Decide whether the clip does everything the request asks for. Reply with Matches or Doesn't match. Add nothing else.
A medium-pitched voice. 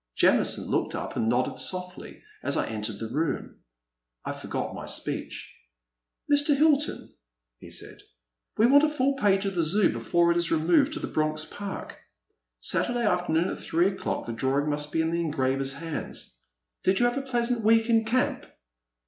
Matches